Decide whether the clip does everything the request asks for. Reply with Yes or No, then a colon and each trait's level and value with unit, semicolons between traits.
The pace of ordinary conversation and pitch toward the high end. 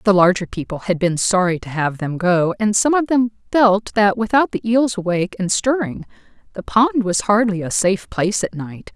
No: fast, 210 wpm; high, 195 Hz